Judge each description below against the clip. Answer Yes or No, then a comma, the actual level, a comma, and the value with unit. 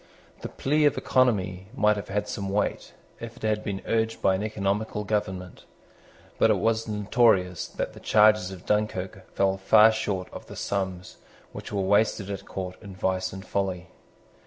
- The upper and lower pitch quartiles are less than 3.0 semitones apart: Yes, narrow, 2.4 semitones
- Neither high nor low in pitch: No, low, 100 Hz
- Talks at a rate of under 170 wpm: No, average, 175 wpm